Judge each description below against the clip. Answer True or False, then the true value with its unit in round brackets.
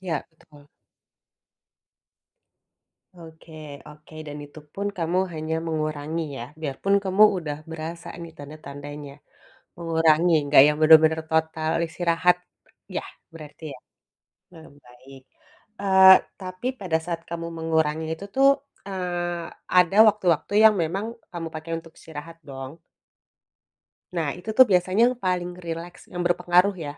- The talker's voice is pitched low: False (165 Hz)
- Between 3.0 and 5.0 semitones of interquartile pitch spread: False (2.4 semitones)